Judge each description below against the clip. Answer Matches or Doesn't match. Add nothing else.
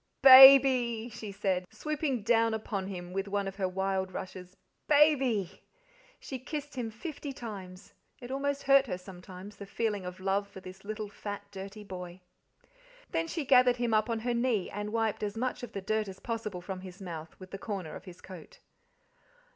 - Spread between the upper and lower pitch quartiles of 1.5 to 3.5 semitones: Doesn't match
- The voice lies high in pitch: Matches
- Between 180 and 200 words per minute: Matches